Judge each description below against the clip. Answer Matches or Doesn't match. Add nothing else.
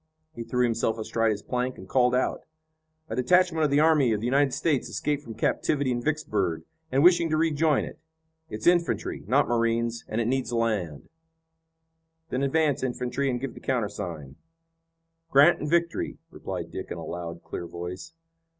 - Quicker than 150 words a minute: Matches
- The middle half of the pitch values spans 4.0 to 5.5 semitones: Matches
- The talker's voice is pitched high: Doesn't match